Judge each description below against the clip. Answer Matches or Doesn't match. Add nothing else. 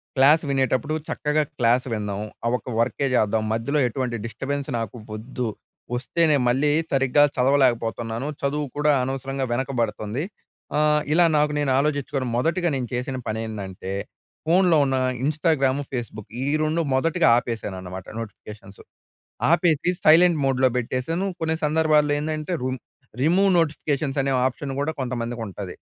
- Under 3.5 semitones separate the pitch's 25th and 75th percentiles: Doesn't match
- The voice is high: Doesn't match